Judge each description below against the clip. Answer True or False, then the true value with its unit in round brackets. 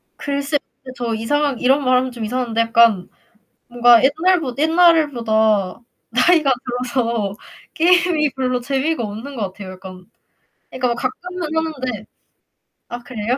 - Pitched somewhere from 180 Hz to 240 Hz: False (255 Hz)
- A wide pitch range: False (4.4 semitones)